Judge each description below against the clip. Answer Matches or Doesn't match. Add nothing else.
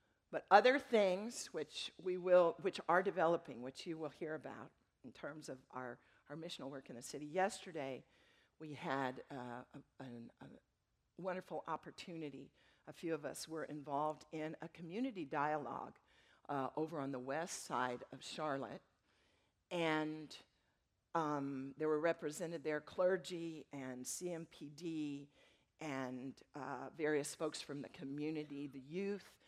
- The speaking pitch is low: Doesn't match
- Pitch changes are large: Doesn't match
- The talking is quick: Doesn't match